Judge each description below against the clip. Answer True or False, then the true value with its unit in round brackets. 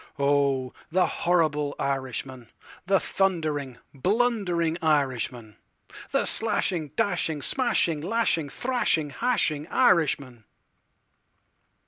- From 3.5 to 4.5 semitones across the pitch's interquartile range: False (5.4 semitones)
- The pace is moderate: False (70 wpm)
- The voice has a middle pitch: True (155 Hz)